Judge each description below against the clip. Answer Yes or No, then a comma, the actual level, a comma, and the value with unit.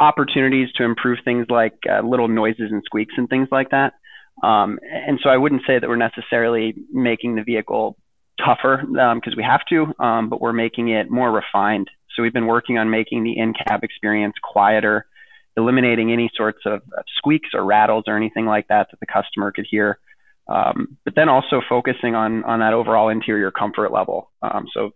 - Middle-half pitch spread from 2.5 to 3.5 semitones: Yes, average, 2.9 semitones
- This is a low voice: Yes, low, 115 Hz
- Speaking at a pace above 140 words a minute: Yes, average, 190 wpm